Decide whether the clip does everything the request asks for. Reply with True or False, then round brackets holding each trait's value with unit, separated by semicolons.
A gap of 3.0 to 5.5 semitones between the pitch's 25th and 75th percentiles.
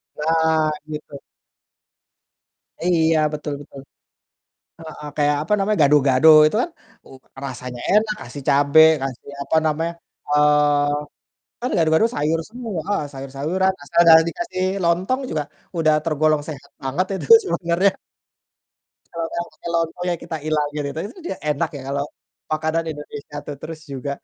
False (2.6 semitones)